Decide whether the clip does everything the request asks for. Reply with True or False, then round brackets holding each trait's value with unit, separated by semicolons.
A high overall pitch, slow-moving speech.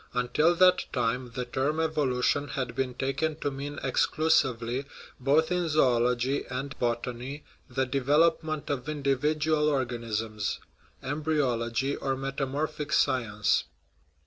False (135 Hz; 120 wpm)